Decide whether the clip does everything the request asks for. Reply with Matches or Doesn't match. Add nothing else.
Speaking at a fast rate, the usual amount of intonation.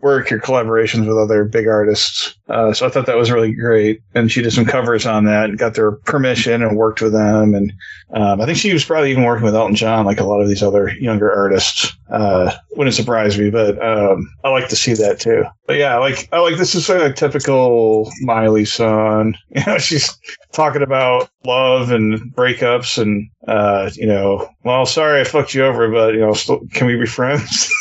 Matches